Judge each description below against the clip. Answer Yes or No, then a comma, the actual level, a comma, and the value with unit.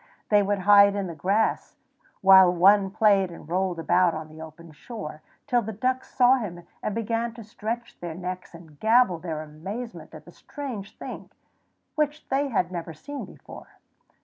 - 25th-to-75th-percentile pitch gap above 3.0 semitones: Yes, average, 4.9 semitones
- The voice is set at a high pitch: Yes, high, 195 Hz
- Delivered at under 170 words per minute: No, average, 175 wpm